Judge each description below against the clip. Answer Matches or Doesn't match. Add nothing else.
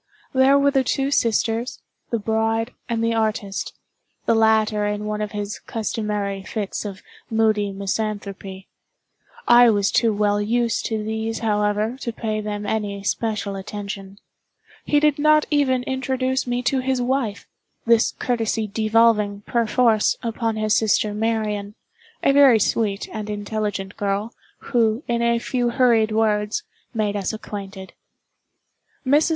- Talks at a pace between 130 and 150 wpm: Matches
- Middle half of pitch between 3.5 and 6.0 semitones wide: Doesn't match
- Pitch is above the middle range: Matches